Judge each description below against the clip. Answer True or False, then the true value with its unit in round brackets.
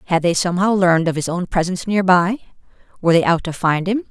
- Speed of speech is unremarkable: False (220 wpm)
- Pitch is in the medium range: True (180 Hz)